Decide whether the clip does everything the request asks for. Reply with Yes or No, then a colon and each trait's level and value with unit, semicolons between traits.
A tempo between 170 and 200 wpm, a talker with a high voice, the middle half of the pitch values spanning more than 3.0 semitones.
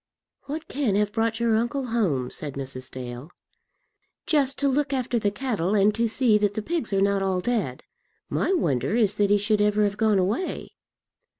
Yes: average, 190 wpm; high, 210 Hz; average, 3.8 semitones